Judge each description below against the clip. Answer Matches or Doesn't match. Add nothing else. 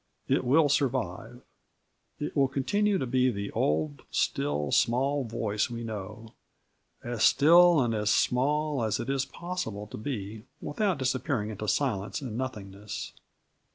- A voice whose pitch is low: Matches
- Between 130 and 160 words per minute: Matches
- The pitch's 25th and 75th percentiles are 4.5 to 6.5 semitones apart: Matches